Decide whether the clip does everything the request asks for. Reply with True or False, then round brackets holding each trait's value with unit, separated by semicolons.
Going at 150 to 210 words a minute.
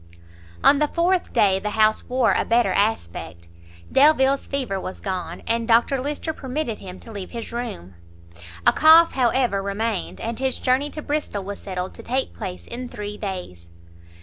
True (170 wpm)